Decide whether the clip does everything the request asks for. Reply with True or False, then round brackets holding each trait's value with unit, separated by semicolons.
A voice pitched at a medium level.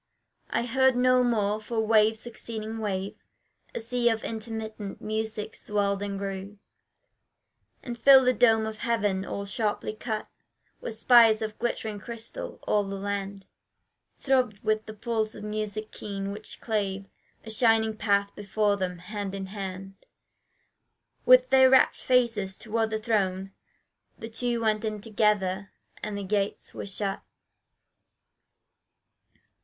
False (215 Hz)